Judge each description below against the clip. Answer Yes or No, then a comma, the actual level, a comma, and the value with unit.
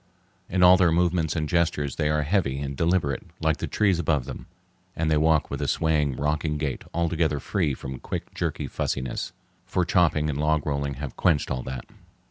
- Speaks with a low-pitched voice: Yes, very low, 75 Hz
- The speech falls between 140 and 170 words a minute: No, average, 190 wpm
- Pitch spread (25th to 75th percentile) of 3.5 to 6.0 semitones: No, average, 3.1 semitones